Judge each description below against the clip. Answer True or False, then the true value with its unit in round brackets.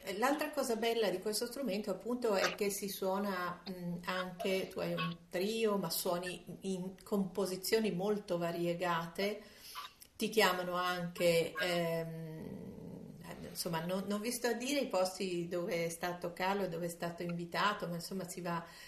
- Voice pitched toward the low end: False (185 Hz)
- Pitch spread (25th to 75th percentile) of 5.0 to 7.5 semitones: False (3.1 semitones)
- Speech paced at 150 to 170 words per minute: True (155 wpm)